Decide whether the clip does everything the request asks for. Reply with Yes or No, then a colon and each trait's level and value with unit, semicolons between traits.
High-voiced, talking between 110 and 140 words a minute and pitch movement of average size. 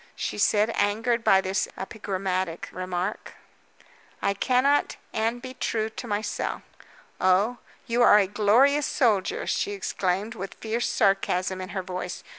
Yes: high, 205 Hz; slow, 135 wpm; average, 4.0 semitones